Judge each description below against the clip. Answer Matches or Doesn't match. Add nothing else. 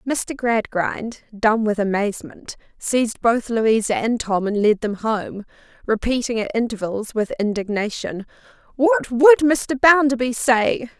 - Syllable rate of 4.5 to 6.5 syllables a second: Doesn't match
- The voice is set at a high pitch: Matches